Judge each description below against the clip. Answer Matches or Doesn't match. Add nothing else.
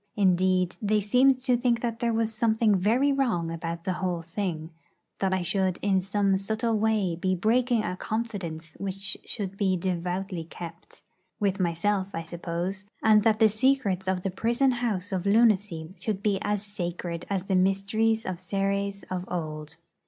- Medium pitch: Doesn't match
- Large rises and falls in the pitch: Doesn't match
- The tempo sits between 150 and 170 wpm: Matches